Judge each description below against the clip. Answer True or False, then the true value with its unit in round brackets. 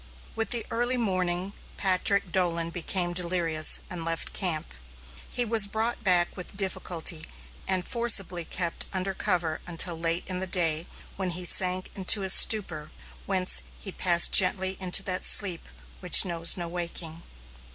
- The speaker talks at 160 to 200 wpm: False (150 wpm)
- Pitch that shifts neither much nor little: False (2.2 semitones)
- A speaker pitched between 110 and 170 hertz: False (180 Hz)